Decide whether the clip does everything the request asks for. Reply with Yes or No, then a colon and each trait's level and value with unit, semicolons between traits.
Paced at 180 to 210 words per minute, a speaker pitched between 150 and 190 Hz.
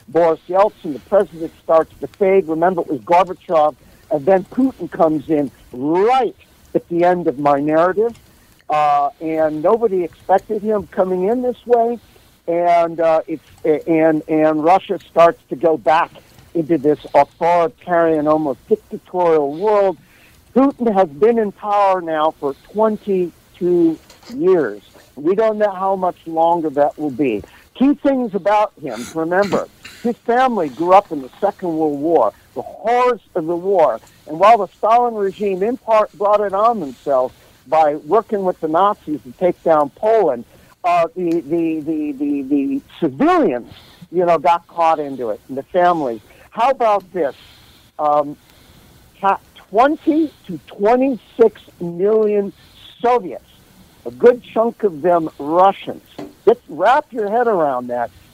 No: average, 145 wpm; medium, 185 Hz